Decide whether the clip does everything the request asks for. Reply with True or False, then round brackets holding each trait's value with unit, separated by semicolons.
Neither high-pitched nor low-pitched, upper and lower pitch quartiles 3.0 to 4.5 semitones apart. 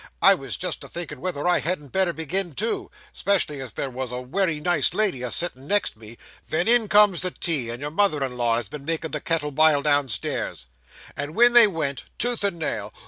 False (155 Hz; 5.6 semitones)